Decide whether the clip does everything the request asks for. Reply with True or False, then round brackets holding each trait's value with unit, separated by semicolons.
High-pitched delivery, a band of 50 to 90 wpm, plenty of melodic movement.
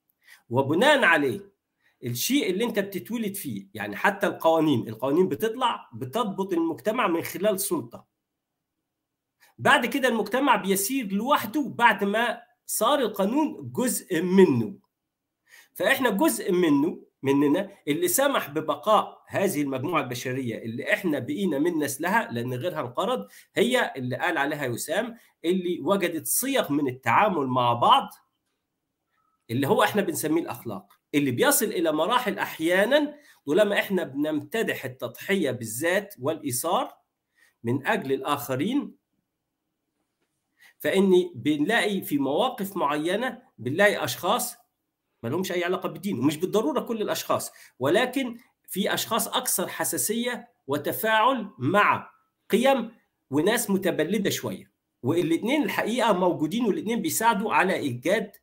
False (195 Hz; 115 wpm; 7.6 semitones)